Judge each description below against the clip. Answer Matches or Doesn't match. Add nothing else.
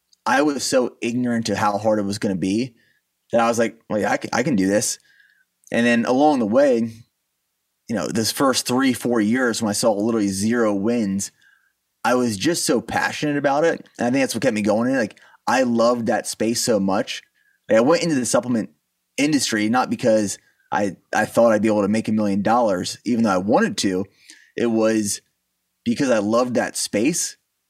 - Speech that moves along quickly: Matches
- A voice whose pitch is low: Matches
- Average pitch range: Doesn't match